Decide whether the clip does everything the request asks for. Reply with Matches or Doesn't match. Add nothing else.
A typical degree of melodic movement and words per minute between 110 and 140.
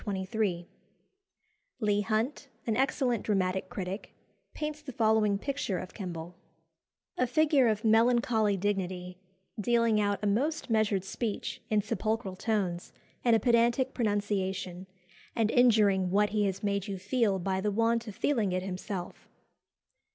Matches